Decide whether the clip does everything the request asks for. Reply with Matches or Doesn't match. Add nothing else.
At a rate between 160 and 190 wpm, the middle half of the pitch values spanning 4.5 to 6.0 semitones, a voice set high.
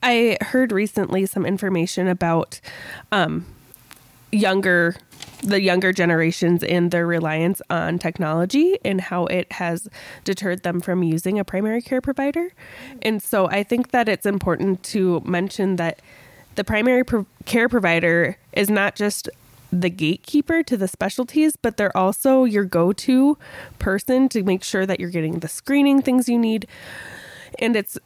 Doesn't match